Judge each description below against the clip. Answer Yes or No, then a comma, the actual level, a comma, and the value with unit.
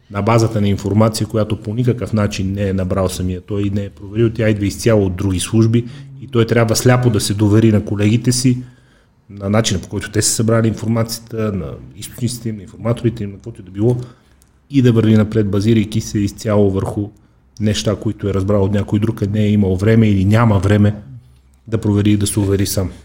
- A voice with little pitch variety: Yes, narrow, 2.1 semitones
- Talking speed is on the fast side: Yes, fast, 210 wpm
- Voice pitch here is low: Yes, low, 105 Hz